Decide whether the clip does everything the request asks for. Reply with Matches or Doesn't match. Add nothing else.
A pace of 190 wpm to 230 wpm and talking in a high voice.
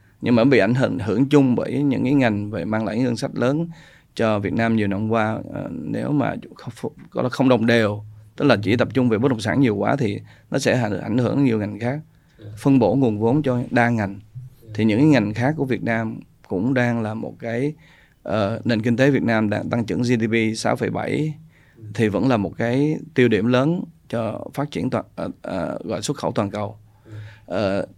Doesn't match